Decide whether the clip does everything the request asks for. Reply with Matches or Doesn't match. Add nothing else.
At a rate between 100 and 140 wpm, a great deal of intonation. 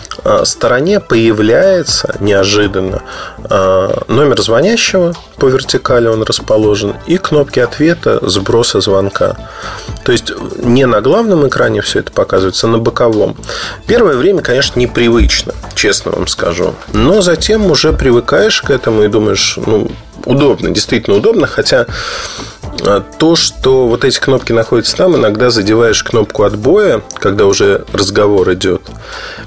Matches